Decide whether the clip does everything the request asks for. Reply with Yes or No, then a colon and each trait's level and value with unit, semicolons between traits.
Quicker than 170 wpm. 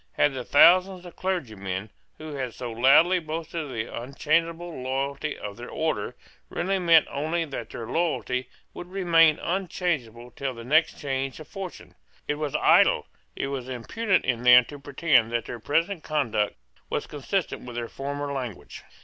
No: average, 165 wpm